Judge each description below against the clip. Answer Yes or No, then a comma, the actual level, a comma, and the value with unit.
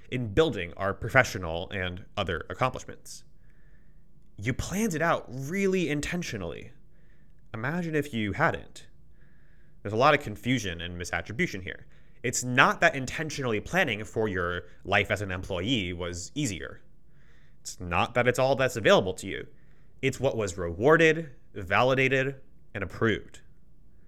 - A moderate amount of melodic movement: No, wide, 6.9 semitones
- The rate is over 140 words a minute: No, slow, 135 wpm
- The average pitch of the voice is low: Yes, low, 125 Hz